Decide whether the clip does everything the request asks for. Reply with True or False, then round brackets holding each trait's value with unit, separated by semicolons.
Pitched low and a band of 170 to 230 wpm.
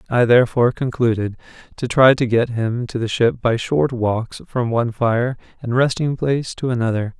True (120 Hz; 185 wpm)